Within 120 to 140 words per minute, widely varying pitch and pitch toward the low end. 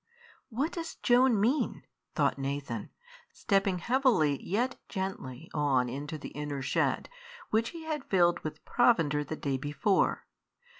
No: slow, 135 wpm; wide, 8.9 semitones; medium, 175 Hz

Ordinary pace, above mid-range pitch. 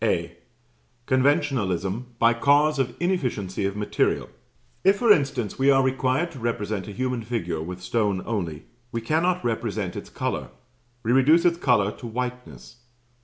No: average, 150 wpm; low, 120 Hz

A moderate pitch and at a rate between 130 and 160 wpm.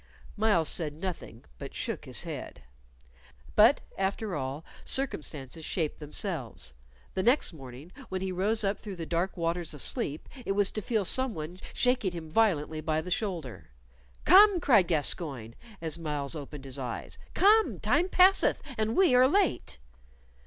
Yes: medium, 175 Hz; average, 155 wpm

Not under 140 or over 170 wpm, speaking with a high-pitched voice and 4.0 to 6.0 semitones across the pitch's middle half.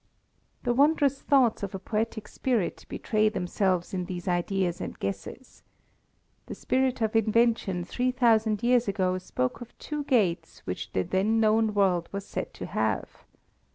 Yes: average, 155 wpm; high, 215 Hz; average, 4.5 semitones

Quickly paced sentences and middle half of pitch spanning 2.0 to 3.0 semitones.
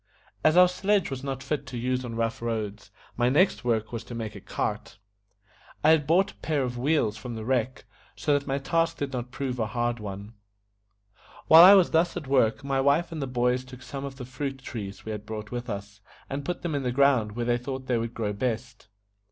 No: fast, 230 wpm; average, 3.5 semitones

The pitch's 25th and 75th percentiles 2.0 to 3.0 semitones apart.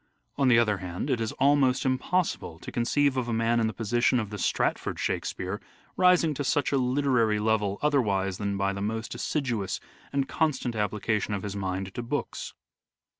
No: average, 4.6 semitones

